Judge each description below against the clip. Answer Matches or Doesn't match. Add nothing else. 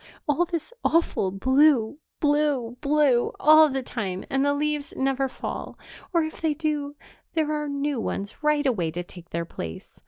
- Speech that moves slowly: Doesn't match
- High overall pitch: Matches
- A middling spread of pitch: Matches